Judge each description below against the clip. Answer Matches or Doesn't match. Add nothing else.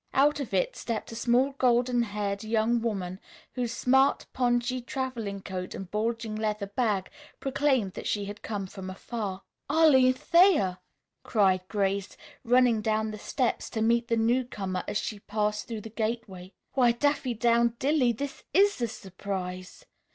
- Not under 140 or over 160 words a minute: Matches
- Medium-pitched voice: Doesn't match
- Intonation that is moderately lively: Matches